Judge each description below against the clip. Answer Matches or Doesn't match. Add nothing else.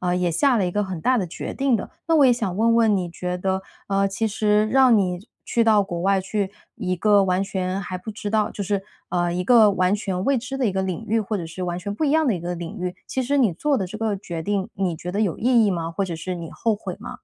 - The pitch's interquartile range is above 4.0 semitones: Doesn't match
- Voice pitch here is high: Matches